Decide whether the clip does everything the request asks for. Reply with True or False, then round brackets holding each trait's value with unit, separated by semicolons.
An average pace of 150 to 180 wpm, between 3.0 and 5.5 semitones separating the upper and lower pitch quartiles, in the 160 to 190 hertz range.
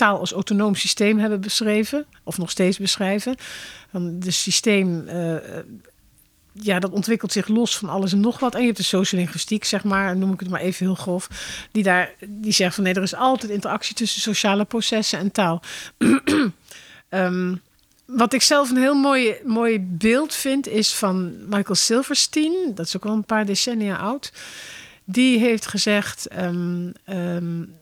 False (170 wpm; 3.6 semitones; 205 Hz)